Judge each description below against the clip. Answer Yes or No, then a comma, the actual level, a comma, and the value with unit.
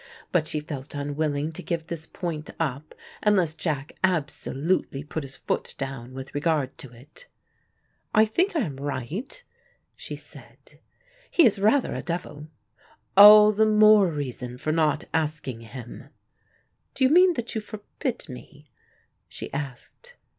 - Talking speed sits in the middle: Yes, average, 145 wpm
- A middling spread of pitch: No, wide, 6.9 semitones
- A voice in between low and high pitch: Yes, medium, 155 Hz